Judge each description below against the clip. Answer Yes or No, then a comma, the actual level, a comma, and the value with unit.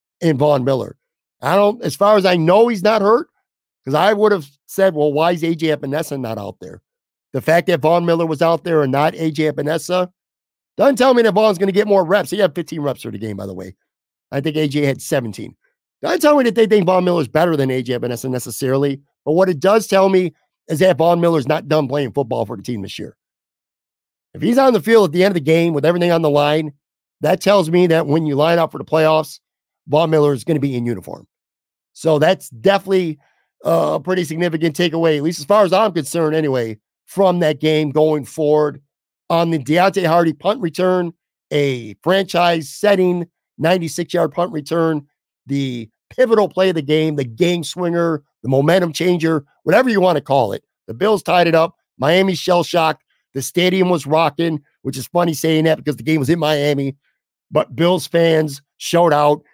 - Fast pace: Yes, fast, 210 wpm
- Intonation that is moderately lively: Yes, average, 3.7 semitones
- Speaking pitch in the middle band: Yes, medium, 165 Hz